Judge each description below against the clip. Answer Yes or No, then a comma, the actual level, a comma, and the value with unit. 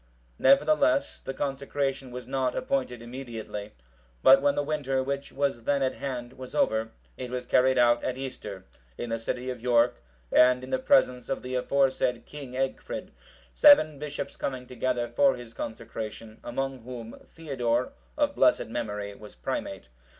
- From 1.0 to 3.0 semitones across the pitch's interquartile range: Yes, narrow, 2.5 semitones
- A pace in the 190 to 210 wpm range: No, average, 155 wpm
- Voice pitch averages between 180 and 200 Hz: No, low, 125 Hz